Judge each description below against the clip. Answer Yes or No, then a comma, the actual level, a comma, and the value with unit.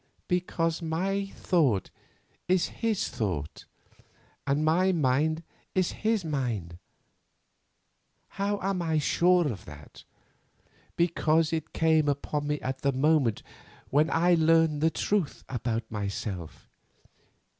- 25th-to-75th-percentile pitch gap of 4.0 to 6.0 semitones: Yes, average, 4.9 semitones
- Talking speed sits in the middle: No, slow, 110 wpm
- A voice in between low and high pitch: Yes, medium, 155 Hz